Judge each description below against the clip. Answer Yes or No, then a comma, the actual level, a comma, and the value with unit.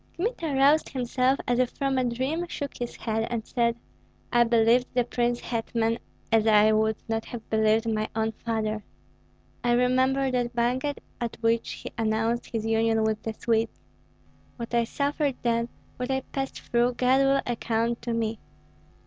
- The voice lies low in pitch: No, high, 235 Hz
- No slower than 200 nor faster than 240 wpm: No, average, 165 wpm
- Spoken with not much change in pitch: Yes, narrow, 2.3 semitones